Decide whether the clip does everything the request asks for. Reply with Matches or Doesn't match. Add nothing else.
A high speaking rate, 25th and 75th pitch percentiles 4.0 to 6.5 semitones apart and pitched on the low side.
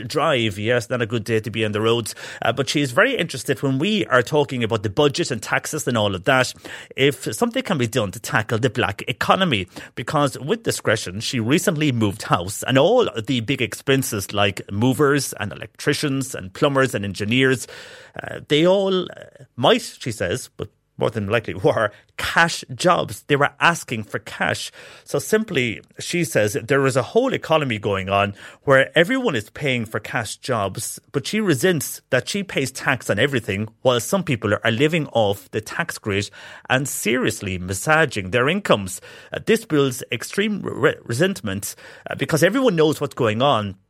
Doesn't match